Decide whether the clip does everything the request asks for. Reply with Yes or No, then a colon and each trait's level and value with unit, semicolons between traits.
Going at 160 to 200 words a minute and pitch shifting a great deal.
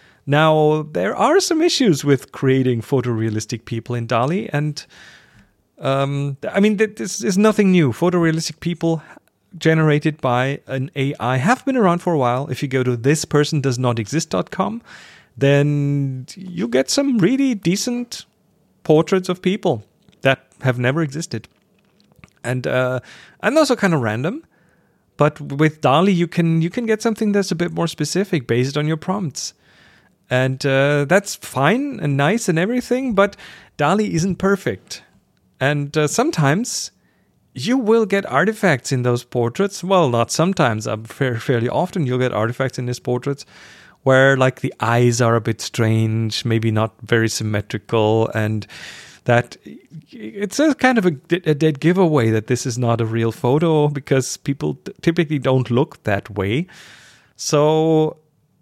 No: average, 150 wpm; wide, 6.5 semitones